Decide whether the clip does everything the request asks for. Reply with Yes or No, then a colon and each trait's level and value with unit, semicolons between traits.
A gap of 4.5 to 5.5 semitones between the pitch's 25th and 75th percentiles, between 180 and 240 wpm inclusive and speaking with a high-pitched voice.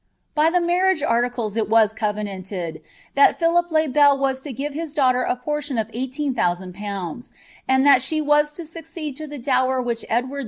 Yes: average, 4.8 semitones; average, 185 wpm; very high, 265 Hz